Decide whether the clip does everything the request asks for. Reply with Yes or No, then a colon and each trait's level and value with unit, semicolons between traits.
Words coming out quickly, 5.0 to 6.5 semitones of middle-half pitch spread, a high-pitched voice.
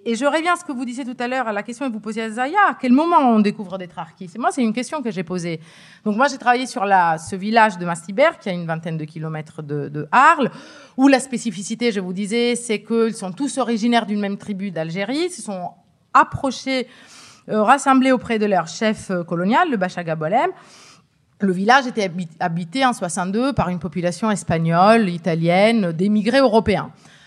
No: average, 205 wpm; wide, 5.6 semitones; high, 215 Hz